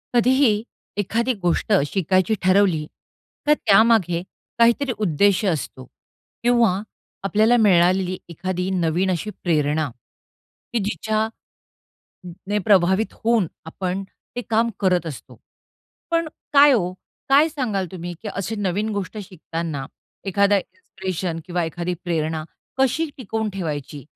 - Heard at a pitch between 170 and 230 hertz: Yes, high, 190 Hz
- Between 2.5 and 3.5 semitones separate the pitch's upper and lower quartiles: No, average, 4.2 semitones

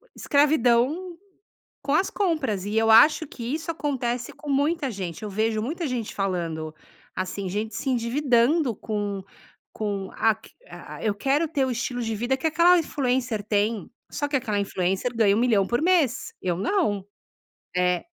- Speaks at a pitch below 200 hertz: No, high, 235 Hz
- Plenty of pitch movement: Yes, wide, 5.9 semitones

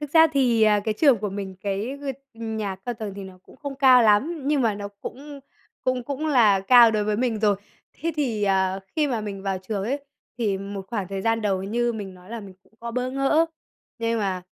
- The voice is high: Yes, high, 220 Hz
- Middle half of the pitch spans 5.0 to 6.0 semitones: No, average, 4.4 semitones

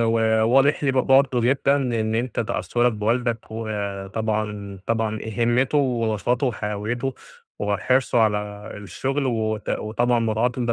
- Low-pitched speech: Yes, low, 115 Hz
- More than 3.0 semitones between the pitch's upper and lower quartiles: No, narrow, 2.5 semitones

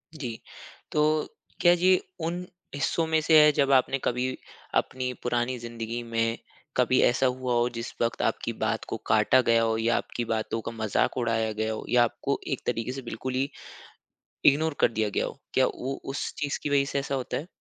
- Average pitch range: Yes, average, 3.2 semitones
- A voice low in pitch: Yes, low, 125 Hz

